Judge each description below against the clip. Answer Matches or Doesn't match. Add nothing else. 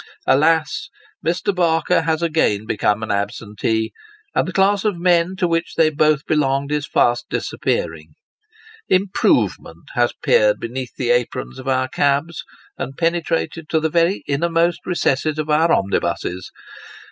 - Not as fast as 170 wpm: Matches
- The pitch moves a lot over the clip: Doesn't match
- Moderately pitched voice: Matches